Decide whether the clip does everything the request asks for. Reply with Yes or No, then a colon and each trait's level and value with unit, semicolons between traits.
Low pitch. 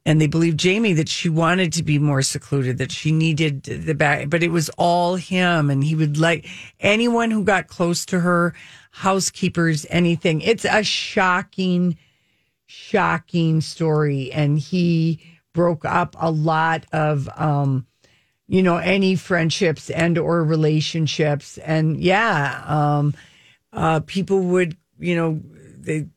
No: medium, 165 Hz